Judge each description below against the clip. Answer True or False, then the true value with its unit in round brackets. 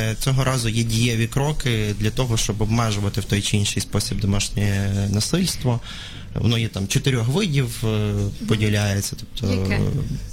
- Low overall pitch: True (110 Hz)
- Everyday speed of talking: True (135 wpm)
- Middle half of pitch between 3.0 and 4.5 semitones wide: True (3.3 semitones)